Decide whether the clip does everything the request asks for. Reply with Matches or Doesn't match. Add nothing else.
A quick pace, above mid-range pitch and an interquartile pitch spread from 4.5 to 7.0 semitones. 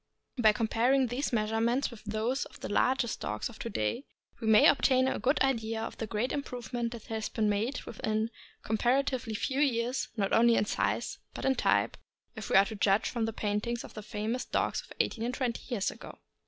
Doesn't match